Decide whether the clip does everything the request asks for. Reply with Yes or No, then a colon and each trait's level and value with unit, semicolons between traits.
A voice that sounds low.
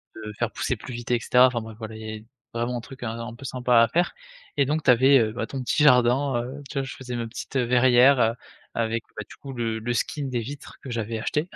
Yes: low, 120 Hz